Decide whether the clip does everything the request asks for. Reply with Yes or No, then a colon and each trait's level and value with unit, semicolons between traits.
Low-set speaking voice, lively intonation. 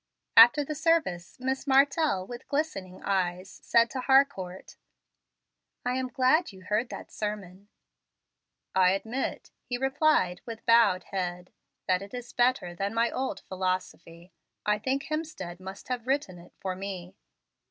No: high, 210 Hz; wide, 6.1 semitones